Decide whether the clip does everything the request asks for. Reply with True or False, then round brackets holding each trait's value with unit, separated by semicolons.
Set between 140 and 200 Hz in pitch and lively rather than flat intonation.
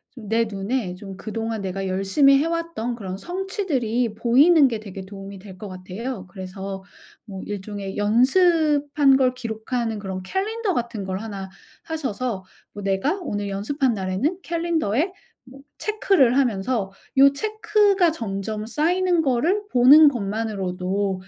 False (230 Hz; 7.1 semitones)